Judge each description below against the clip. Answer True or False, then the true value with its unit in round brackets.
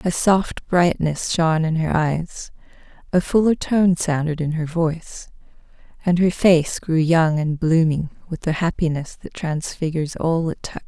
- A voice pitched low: False (165 Hz)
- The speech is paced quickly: False (160 wpm)